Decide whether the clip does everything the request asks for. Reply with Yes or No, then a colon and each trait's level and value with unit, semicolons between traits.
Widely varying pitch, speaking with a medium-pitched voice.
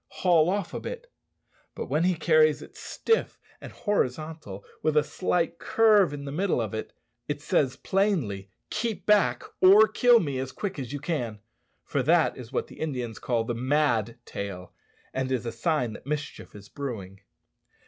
Yes: wide, 6.8 semitones; medium, 150 Hz